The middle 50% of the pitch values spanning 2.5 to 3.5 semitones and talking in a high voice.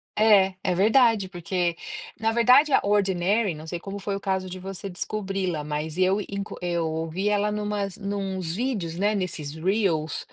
Yes: average, 2.9 semitones; high, 195 Hz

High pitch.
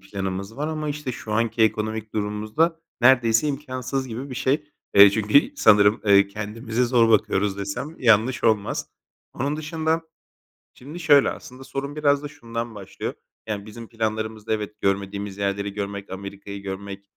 No: low, 110 Hz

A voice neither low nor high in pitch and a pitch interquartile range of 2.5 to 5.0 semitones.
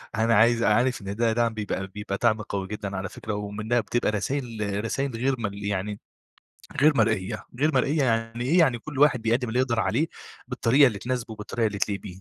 No: low, 115 Hz; average, 3.2 semitones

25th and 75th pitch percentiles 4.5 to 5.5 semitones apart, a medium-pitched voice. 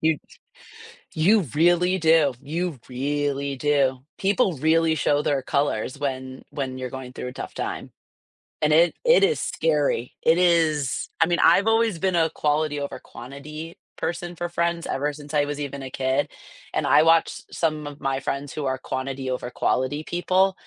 No: average, 3.6 semitones; medium, 150 Hz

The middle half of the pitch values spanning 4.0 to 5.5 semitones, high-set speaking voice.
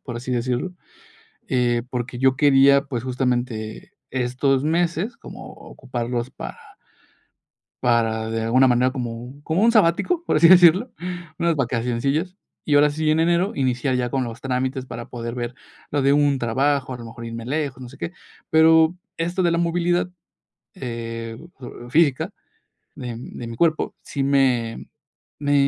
No: average, 4.6 semitones; low, 130 Hz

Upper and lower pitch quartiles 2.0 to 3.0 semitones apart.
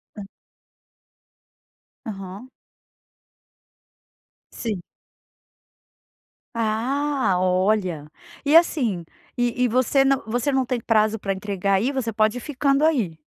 No: average, 5.1 semitones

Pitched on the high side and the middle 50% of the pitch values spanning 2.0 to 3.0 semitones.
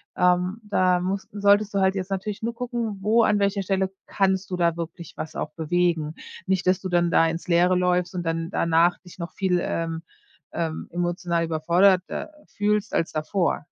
No: medium, 180 Hz; narrow, 2.5 semitones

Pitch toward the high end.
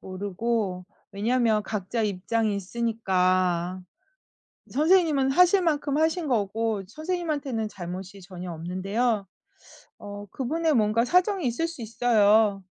Yes: high, 225 Hz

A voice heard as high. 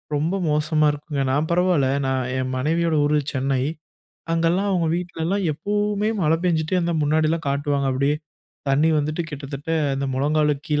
No: medium, 155 Hz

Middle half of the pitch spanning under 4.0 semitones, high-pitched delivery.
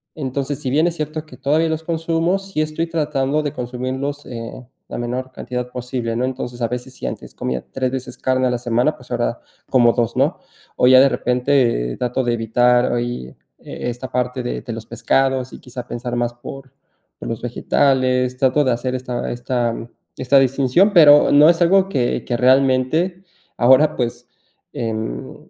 No: average, 2.8 semitones; low, 130 Hz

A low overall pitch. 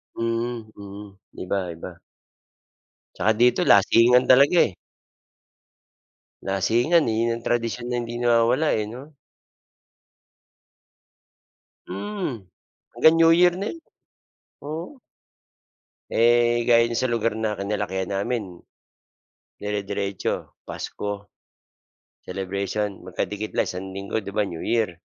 Yes: low, 115 Hz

